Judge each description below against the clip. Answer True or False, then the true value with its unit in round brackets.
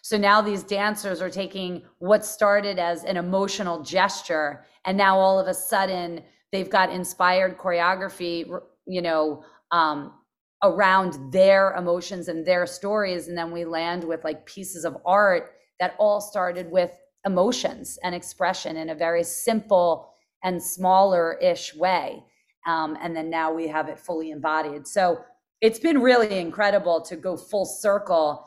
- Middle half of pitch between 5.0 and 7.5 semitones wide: False (2.8 semitones)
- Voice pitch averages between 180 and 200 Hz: True (185 Hz)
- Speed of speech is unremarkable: True (155 wpm)